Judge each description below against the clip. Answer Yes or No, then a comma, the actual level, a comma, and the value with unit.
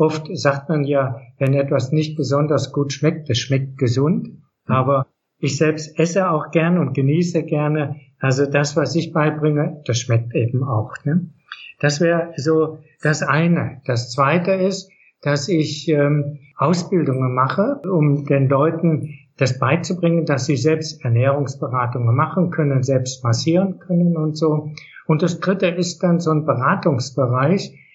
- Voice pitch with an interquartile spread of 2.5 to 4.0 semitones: Yes, average, 3.2 semitones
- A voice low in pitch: No, medium, 150 Hz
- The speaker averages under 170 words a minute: Yes, average, 150 wpm